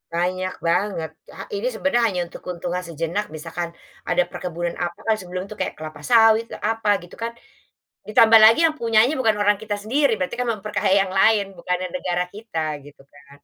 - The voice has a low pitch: No, high, 195 Hz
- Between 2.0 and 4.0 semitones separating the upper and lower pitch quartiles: No, average, 4.4 semitones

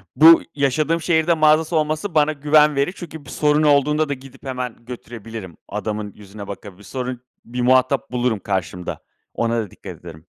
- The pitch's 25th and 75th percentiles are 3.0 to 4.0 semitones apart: No, wide, 5.6 semitones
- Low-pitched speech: Yes, low, 130 Hz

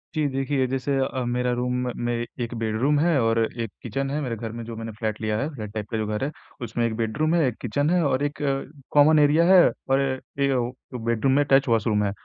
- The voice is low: Yes, low, 125 Hz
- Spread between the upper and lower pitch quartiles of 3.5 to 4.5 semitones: Yes, average, 3.9 semitones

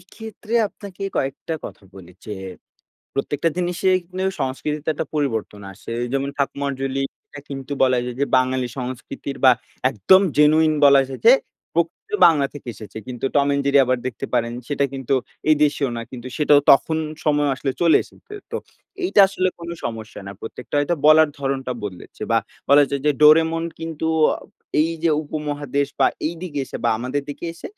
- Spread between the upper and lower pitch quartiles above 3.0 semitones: Yes, average, 3.5 semitones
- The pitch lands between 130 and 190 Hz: Yes, medium, 140 Hz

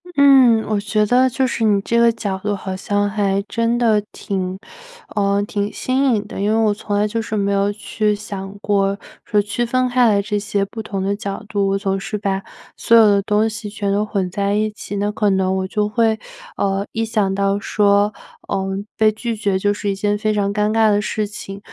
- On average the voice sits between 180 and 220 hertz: Yes, high, 205 Hz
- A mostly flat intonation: Yes, narrow, 1.7 semitones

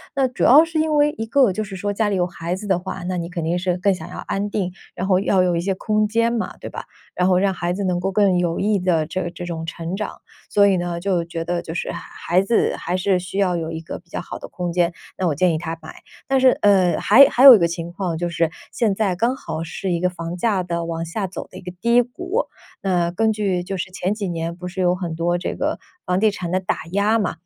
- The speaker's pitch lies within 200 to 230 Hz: No, medium, 185 Hz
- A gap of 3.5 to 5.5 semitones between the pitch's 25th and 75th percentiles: No, average, 2.9 semitones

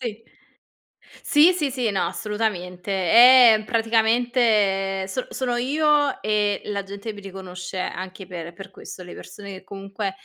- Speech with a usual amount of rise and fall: Yes, average, 3.8 semitones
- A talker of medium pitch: No, high, 210 Hz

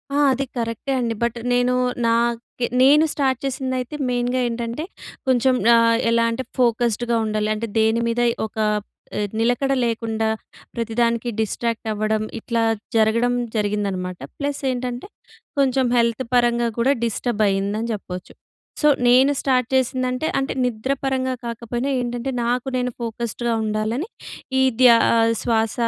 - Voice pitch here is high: Yes, high, 235 Hz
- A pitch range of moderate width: No, narrow, 2.0 semitones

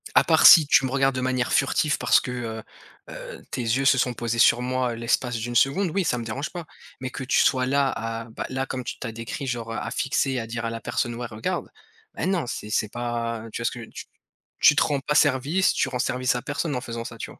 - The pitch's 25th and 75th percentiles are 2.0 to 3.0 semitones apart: Yes, average, 2.7 semitones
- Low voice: Yes, low, 125 Hz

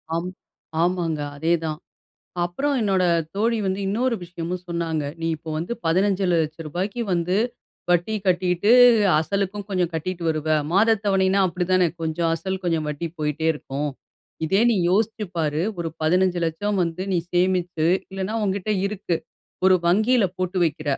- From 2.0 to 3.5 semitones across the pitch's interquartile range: Yes, average, 3.0 semitones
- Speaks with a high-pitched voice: No, medium, 180 Hz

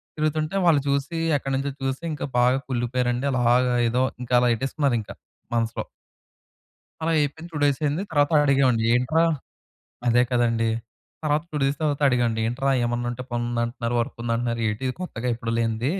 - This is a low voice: Yes, low, 125 Hz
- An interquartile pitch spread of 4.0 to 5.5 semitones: No, average, 3.1 semitones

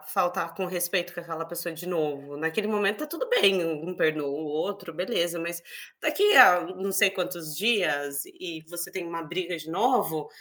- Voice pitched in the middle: Yes, medium, 175 Hz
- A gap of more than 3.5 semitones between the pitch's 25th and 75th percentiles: No, average, 2.7 semitones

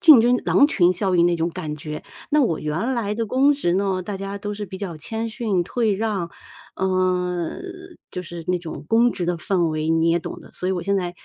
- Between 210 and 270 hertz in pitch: No, medium, 185 Hz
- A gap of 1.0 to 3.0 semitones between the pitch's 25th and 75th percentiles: No, average, 4.1 semitones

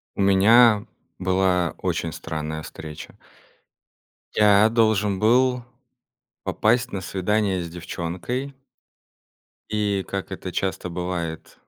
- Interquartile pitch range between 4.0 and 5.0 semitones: No, average, 3.5 semitones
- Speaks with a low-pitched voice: Yes, very low, 95 Hz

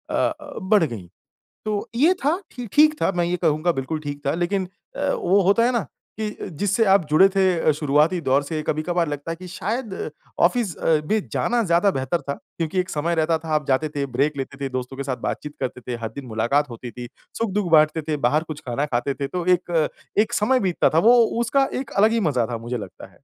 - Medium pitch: Yes, medium, 160 Hz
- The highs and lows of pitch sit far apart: Yes, wide, 6.3 semitones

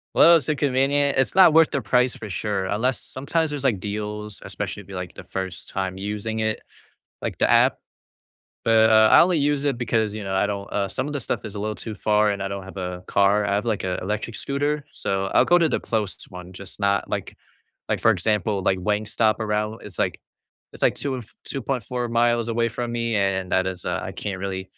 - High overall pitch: No, low, 110 Hz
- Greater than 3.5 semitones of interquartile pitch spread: Yes, average, 4.1 semitones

